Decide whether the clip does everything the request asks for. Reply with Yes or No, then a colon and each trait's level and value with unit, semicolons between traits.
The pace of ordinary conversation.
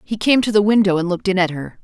No: fast, 325 wpm